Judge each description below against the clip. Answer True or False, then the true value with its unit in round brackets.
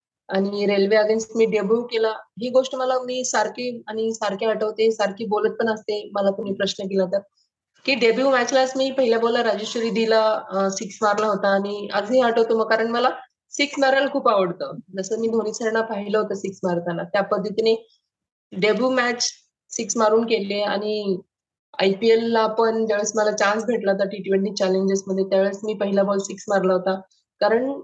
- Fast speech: True (170 wpm)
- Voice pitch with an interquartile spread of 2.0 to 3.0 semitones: True (2.4 semitones)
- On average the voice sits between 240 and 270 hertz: False (215 Hz)